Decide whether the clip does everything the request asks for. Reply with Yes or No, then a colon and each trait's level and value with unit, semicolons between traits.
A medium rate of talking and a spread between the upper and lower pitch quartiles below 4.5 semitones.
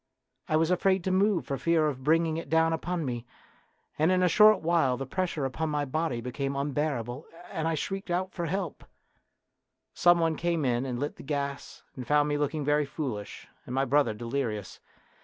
Yes: average, 195 wpm; average, 3.7 semitones